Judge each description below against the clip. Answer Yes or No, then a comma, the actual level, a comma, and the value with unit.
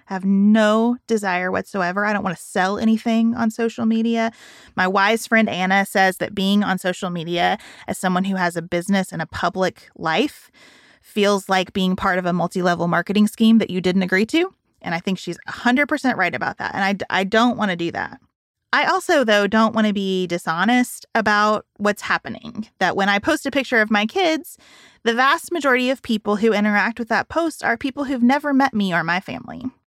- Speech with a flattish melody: No, average, 3.8 semitones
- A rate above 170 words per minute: Yes, fast, 205 wpm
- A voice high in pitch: Yes, high, 210 Hz